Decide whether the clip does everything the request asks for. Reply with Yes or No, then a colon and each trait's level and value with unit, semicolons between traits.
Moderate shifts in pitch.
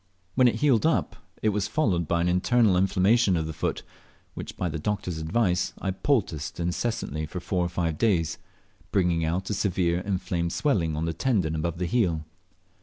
Yes: average, 3.9 semitones